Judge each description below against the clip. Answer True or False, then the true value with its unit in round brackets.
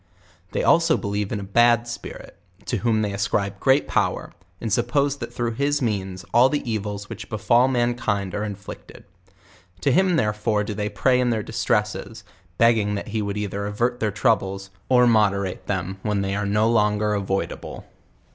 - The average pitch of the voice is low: True (105 Hz)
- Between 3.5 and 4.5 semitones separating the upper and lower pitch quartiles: False (2.9 semitones)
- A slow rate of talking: False (180 wpm)